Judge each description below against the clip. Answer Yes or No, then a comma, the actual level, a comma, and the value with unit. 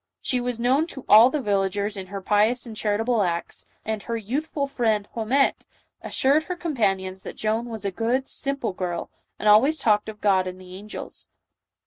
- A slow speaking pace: No, average, 185 wpm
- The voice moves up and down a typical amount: Yes, average, 4.0 semitones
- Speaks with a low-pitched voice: No, high, 220 Hz